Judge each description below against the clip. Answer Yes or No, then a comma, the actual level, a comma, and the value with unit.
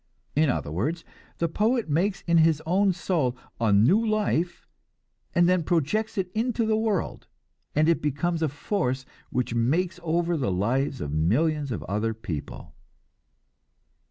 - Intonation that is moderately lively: No, wide, 6.4 semitones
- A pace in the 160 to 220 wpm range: No, average, 150 wpm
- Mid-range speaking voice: Yes, medium, 160 Hz